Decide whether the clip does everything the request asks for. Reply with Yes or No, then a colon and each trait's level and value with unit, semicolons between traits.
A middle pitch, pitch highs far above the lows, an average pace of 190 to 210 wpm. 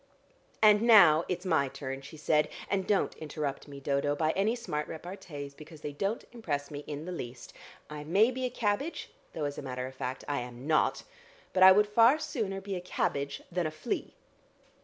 Yes: medium, 155 Hz; wide, 5.8 semitones; average, 200 wpm